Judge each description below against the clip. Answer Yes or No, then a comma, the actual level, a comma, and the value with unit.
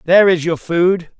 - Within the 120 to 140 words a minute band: No, average, 200 wpm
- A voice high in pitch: No, medium, 175 Hz